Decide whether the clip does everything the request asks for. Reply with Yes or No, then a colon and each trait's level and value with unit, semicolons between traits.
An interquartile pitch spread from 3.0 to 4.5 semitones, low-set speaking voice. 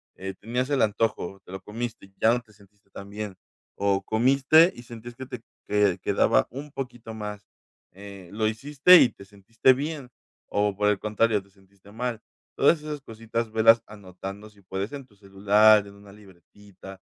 Yes: average, 3.4 semitones; low, 105 Hz